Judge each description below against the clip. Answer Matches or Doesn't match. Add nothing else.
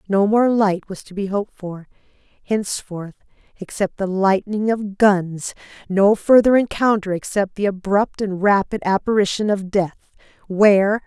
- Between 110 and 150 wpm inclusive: Matches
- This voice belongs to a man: Doesn't match